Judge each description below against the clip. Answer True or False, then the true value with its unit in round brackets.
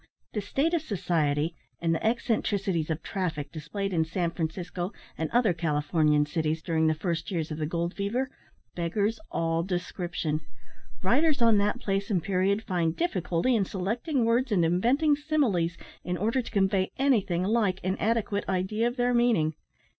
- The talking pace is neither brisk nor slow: True (160 wpm)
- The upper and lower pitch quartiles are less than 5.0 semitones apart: False (5.4 semitones)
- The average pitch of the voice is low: False (185 Hz)